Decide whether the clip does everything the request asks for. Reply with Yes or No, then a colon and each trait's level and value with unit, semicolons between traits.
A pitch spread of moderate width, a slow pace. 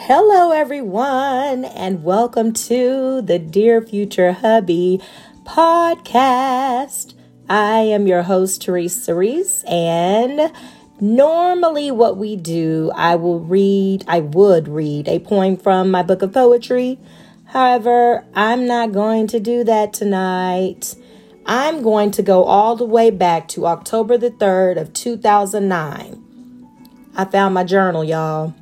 Yes: average, 5.0 semitones; slow, 130 wpm